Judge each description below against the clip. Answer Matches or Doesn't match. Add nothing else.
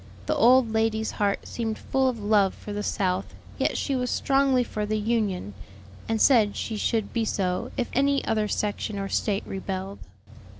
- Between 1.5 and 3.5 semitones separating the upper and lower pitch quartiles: Matches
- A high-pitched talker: Matches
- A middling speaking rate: Matches